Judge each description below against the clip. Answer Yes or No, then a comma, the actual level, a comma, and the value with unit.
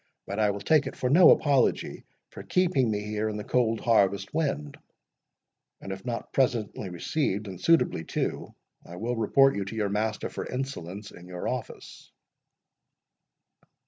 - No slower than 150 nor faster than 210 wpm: Yes, average, 160 wpm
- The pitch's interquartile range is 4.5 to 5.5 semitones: Yes, average, 4.9 semitones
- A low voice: Yes, low, 110 Hz